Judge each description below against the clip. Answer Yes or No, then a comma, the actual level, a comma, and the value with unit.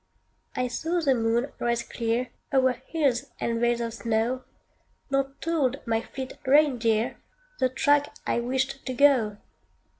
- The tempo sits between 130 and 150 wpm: Yes, average, 140 wpm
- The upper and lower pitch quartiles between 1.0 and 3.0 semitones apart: Yes, narrow, 2.6 semitones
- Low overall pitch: No, very high, 255 Hz